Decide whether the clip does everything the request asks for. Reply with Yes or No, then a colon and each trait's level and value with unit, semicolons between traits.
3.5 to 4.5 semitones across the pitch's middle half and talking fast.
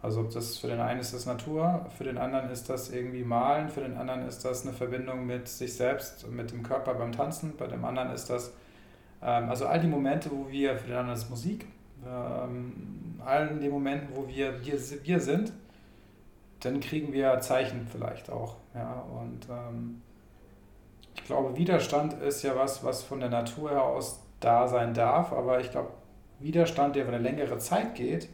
No: average, 2.7 semitones; fast, 195 wpm